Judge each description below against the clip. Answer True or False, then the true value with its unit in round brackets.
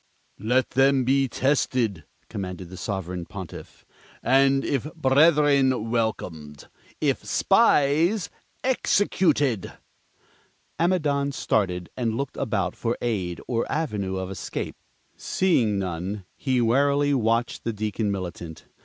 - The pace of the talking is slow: True (110 wpm)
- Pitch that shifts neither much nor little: False (6.3 semitones)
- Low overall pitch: True (120 Hz)